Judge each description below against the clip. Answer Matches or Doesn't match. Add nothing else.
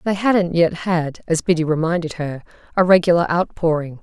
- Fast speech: Doesn't match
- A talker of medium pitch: Matches